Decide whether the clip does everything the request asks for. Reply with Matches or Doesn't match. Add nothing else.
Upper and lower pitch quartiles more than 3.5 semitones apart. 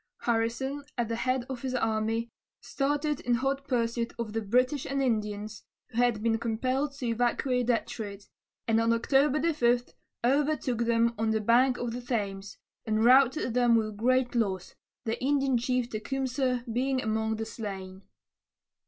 Doesn't match